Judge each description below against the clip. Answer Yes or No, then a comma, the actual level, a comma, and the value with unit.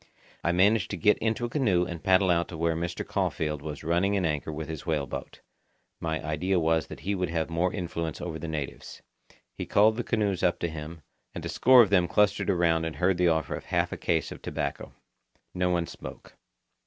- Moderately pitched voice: No, very low, 85 Hz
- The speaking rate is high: Yes, fast, 215 wpm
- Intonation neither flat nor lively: Yes, average, 3.0 semitones